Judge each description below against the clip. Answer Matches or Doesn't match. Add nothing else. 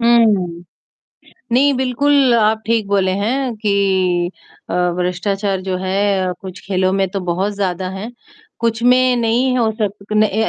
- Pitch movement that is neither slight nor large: Matches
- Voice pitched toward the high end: Matches